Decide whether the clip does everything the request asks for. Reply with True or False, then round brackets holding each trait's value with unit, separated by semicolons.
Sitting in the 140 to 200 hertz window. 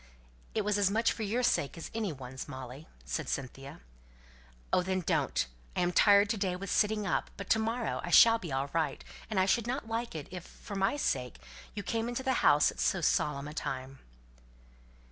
True (190 Hz)